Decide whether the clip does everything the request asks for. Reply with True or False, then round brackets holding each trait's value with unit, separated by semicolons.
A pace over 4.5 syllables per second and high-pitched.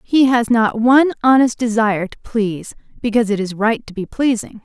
True (5.5 syllables/s; 230 Hz)